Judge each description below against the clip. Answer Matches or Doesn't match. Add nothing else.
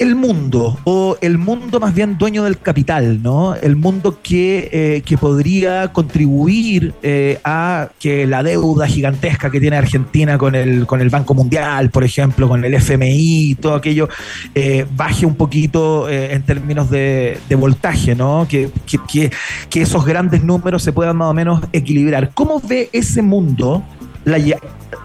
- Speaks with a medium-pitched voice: Matches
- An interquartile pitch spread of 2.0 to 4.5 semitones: Matches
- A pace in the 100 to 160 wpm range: Doesn't match